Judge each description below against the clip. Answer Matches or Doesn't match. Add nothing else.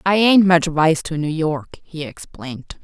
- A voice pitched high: Doesn't match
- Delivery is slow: Doesn't match